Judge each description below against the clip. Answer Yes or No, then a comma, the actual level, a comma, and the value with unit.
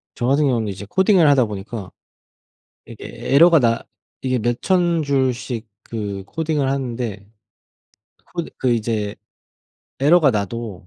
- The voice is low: Yes, low, 125 Hz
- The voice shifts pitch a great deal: No, average, 5.0 semitones